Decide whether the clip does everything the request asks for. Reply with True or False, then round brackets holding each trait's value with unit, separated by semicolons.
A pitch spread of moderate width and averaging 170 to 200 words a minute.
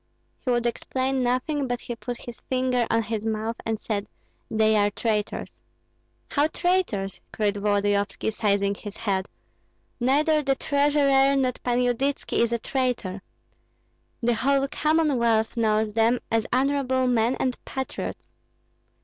False (3.6 semitones; 135 wpm)